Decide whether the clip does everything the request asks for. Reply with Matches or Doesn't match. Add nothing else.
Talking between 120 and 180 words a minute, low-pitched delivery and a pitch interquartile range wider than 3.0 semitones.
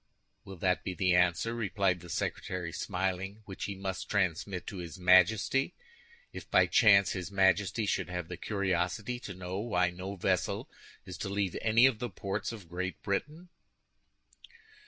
Doesn't match